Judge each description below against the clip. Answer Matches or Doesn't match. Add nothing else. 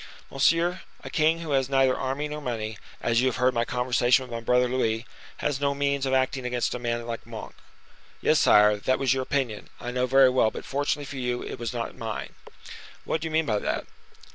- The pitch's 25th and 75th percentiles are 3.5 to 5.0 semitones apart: Doesn't match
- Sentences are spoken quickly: Matches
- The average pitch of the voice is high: Doesn't match